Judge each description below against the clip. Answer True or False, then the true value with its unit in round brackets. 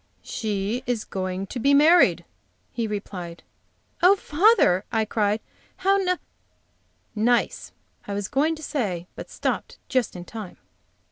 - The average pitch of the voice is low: False (220 Hz)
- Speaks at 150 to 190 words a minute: False (140 wpm)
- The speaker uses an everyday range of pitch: False (7.0 semitones)